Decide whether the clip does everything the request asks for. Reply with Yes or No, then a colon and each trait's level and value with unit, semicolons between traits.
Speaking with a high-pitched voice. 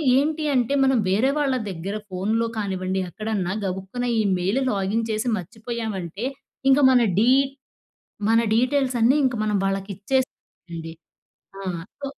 Yes: high, 220 Hz